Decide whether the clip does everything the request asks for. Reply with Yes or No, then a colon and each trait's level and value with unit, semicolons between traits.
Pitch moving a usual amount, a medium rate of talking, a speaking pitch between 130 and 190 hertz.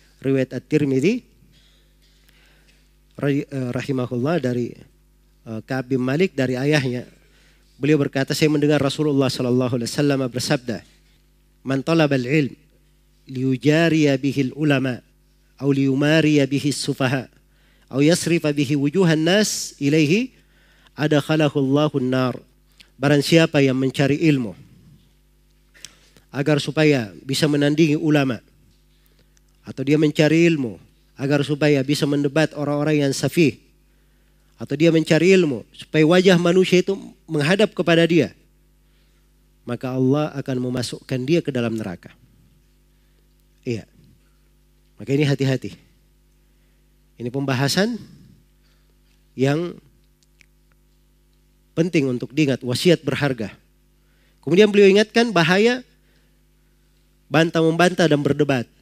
Yes: average, 3.4 semitones; average, 105 wpm; medium, 140 Hz